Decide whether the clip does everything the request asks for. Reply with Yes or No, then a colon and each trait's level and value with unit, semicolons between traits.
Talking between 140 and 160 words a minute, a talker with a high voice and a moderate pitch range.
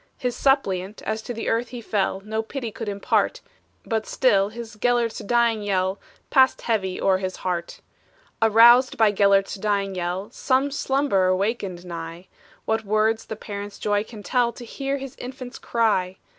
Yes: average, 155 wpm; high, 215 Hz; average, 3.5 semitones